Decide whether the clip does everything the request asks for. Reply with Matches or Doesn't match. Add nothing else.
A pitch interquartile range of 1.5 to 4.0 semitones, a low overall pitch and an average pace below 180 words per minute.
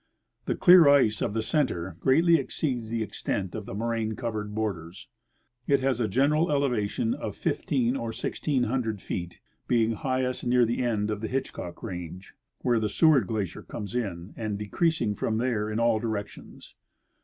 Matches